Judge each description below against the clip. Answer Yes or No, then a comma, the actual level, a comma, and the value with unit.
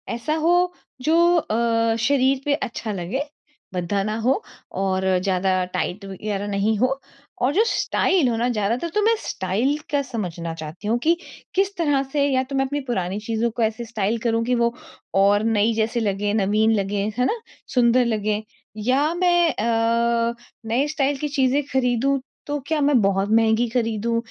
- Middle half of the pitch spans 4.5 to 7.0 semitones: Yes, average, 4.8 semitones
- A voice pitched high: Yes, high, 235 Hz